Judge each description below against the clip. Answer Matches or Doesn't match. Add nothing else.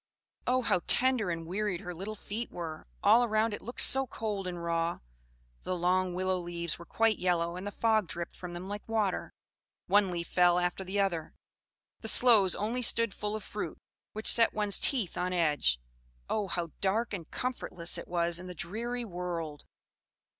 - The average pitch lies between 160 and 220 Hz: Matches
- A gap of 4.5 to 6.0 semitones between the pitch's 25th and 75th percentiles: Doesn't match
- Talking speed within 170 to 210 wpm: Matches